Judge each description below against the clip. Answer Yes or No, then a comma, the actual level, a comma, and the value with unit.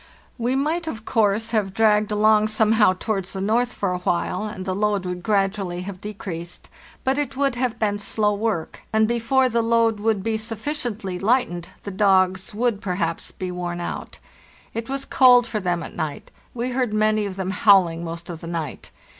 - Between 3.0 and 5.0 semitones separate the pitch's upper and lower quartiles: Yes, average, 3.5 semitones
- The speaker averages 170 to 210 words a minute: Yes, average, 190 wpm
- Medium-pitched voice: No, high, 210 Hz